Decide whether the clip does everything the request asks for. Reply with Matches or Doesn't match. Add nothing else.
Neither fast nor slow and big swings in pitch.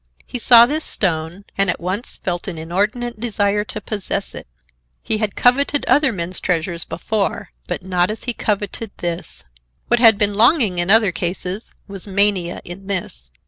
Doesn't match